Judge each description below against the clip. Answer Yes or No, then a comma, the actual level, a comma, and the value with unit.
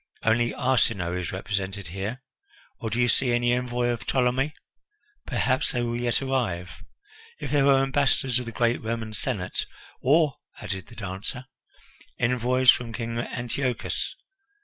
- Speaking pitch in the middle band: No, low, 120 Hz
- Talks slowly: No, average, 150 wpm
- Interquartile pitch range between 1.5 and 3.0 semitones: Yes, average, 2.7 semitones